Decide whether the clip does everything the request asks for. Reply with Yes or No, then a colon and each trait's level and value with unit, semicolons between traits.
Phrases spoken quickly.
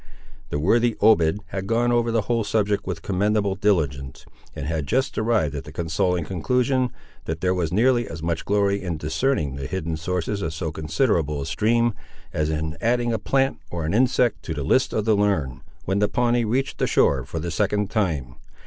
No: average, 195 wpm